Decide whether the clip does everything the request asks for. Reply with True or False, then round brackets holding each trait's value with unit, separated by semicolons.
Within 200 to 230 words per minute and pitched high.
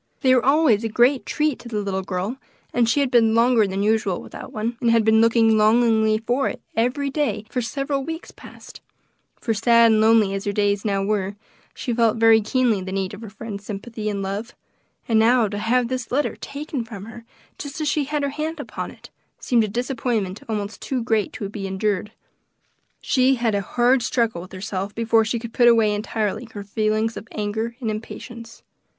True (205 wpm; 225 Hz)